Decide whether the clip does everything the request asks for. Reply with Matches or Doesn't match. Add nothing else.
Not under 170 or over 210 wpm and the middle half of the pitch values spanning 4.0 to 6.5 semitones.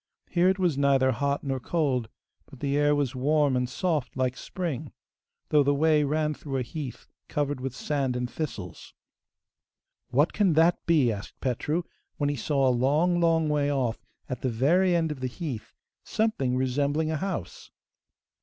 Doesn't match